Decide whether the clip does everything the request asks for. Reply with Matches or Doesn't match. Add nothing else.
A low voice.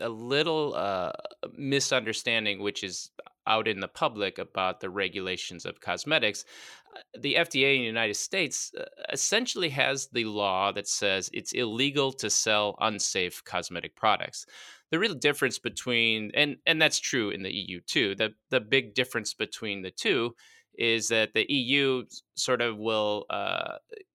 Matches